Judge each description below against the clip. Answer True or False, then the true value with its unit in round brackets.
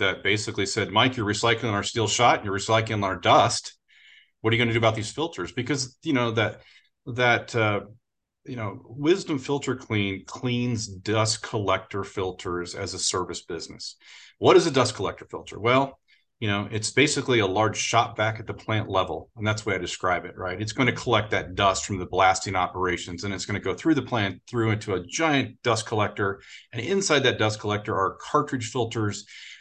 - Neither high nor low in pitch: False (110 Hz)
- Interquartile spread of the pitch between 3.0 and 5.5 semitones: True (3.4 semitones)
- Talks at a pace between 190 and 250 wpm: True (205 wpm)